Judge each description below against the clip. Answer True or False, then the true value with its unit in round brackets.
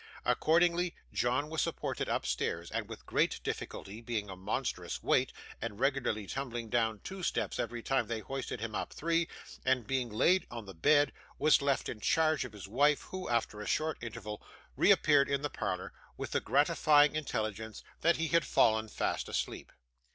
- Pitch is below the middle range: True (130 Hz)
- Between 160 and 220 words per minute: True (170 wpm)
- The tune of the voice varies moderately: False (5.7 semitones)